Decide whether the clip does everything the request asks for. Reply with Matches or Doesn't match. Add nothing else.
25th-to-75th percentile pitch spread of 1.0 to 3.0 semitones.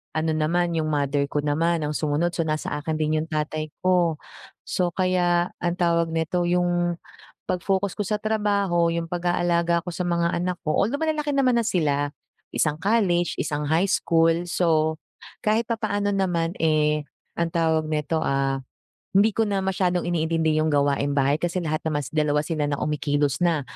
Matches